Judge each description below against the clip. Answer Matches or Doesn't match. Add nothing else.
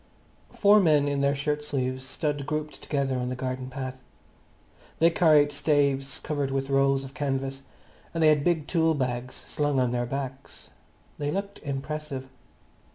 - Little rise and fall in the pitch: Matches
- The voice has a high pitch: Doesn't match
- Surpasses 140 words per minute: Matches